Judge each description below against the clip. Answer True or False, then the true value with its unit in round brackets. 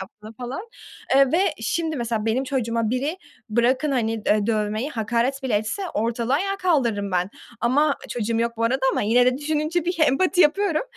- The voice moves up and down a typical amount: True (5.0 semitones)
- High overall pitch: True (250 Hz)